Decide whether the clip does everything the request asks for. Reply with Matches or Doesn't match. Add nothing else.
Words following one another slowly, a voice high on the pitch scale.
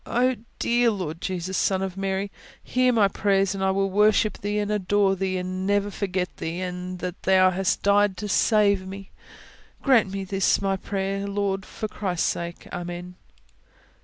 Doesn't match